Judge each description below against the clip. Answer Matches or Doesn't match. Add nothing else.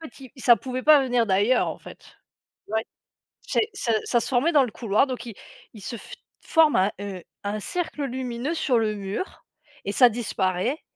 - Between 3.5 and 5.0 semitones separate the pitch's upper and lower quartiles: Matches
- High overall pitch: Matches